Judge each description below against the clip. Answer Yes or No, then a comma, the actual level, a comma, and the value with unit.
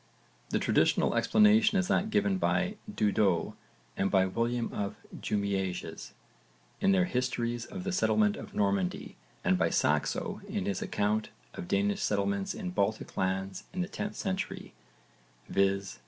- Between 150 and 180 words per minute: No, average, 140 wpm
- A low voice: Yes, low, 110 Hz